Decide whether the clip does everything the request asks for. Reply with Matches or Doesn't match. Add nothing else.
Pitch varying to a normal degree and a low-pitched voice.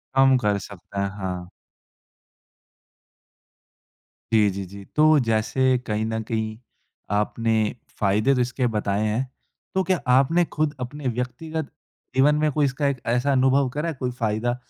Matches